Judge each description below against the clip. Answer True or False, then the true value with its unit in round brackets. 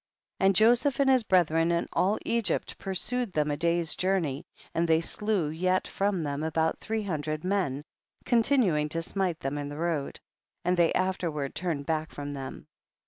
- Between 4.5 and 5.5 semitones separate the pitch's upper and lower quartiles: False (4.1 semitones)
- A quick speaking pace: False (175 wpm)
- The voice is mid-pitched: True (170 Hz)